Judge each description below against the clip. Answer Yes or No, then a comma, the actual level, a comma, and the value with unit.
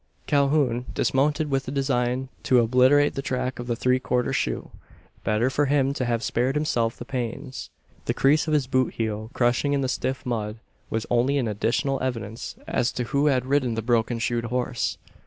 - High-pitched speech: No, low, 125 Hz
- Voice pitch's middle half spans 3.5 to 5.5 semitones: No, narrow, 2.5 semitones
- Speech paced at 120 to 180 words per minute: No, average, 190 wpm